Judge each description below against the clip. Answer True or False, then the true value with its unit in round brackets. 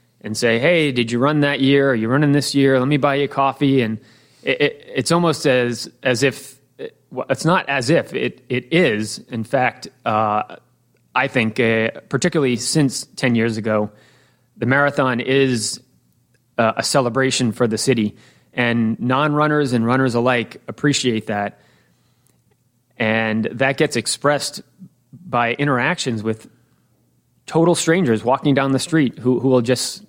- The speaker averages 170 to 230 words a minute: False (160 wpm)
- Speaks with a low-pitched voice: True (130 Hz)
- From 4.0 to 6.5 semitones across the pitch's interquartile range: False (3.6 semitones)